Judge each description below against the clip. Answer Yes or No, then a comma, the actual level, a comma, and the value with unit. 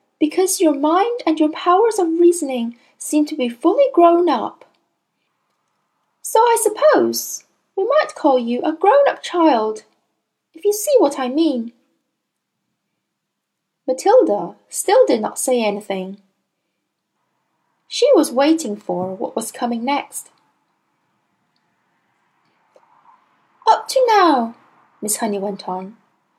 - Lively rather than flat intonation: Yes, wide, 8.1 semitones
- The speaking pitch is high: Yes, very high, 305 Hz